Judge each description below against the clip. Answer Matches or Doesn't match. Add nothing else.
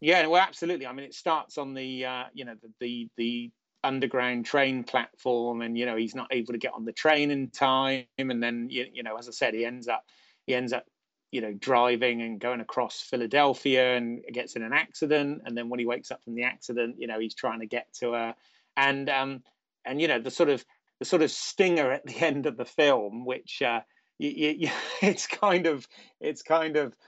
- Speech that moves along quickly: Matches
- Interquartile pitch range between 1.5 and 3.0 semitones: Matches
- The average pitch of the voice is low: Matches